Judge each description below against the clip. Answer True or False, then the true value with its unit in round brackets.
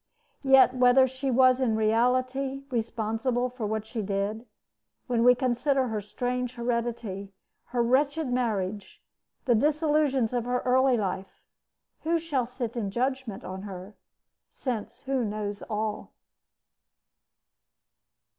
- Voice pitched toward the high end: True (245 Hz)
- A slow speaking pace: True (120 wpm)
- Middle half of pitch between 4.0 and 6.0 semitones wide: False (3.2 semitones)